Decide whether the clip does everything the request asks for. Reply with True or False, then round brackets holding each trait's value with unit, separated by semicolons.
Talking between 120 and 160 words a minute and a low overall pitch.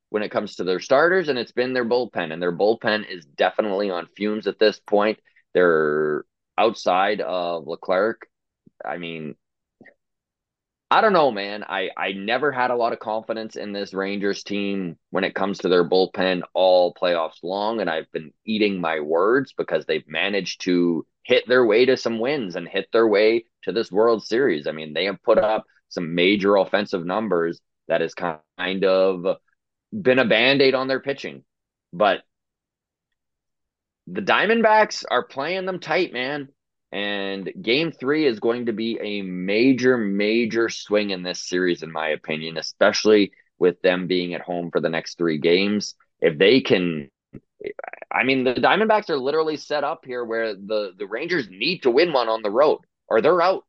False (175 wpm; 100 Hz)